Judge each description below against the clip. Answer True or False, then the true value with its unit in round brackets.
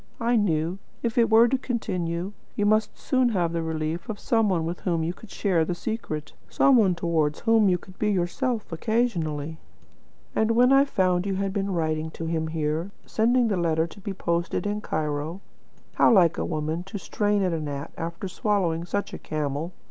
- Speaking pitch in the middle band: True (180 Hz)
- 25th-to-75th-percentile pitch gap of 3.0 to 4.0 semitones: False (4.9 semitones)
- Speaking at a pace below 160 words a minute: False (195 wpm)